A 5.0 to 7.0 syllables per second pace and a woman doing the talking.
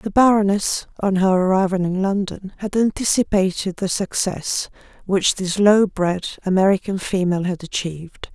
No: 4.8 syllables/s; female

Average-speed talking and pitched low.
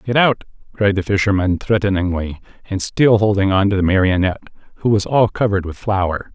Yes: average, 170 wpm; low, 100 Hz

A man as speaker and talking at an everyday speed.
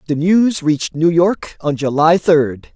Yes: male; average, 175 wpm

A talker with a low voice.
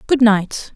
No: high, 225 Hz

